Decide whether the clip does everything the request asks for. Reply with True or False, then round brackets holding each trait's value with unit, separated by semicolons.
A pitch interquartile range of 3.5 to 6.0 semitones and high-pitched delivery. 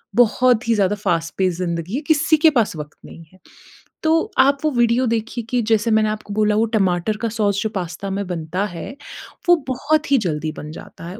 True (5.2 semitones; 215 Hz)